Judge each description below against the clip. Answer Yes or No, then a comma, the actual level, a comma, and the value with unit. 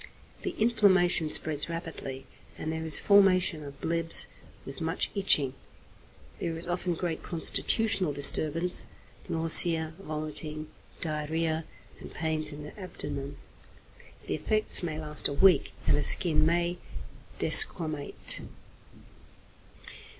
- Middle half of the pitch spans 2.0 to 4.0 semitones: Yes, narrow, 2.5 semitones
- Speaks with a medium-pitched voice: Yes, medium, 160 Hz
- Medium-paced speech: No, slow, 115 wpm